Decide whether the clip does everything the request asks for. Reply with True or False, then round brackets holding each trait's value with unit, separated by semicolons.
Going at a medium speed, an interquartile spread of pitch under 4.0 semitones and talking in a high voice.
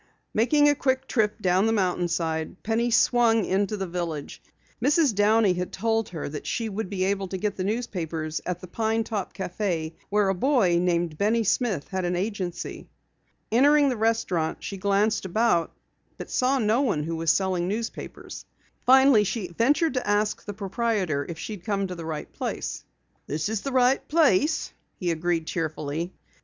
False (175 wpm; 4.4 semitones; 200 Hz)